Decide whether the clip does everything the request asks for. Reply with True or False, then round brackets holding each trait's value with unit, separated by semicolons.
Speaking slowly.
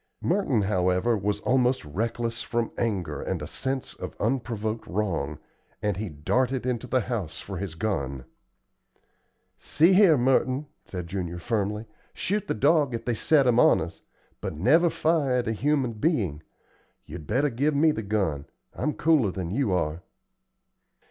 False (160 wpm)